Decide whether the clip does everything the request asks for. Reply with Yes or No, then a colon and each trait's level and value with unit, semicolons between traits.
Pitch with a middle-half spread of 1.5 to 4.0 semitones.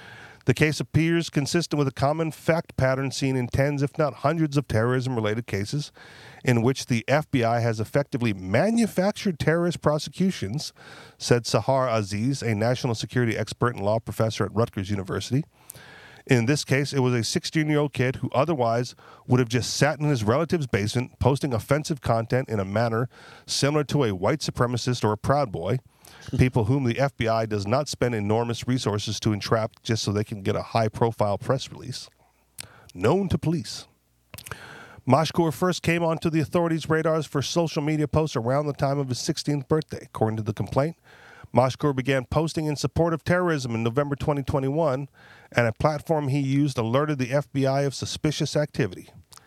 No: average, 4.4 semitones